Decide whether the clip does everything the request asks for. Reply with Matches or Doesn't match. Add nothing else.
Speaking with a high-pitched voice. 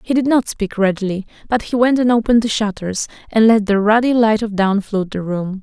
Matches